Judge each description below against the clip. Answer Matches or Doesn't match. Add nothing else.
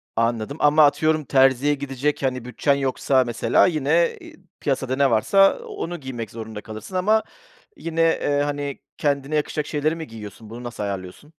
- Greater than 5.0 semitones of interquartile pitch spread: Doesn't match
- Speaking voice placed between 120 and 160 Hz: Matches